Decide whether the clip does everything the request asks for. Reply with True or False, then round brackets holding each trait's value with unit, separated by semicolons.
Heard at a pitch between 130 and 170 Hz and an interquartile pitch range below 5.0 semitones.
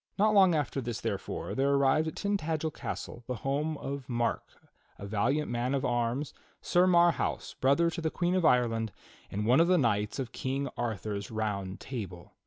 False (135 Hz; 5.5 semitones)